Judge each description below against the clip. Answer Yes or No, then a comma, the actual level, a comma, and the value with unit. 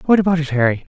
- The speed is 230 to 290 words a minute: Yes, fast, 255 wpm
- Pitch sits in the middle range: Yes, medium, 160 Hz